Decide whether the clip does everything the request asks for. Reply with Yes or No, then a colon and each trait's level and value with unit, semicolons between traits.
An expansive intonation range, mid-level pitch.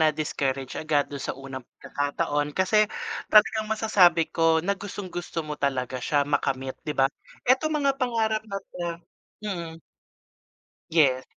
Yes: wide, 6.5 semitones; medium, 160 Hz